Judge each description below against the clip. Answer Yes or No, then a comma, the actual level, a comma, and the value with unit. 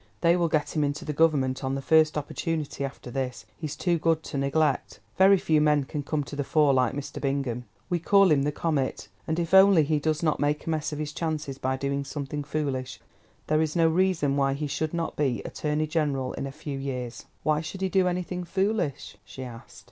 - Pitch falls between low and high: Yes, medium, 150 Hz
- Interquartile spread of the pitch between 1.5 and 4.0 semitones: Yes, average, 2.9 semitones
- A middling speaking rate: No, fast, 220 wpm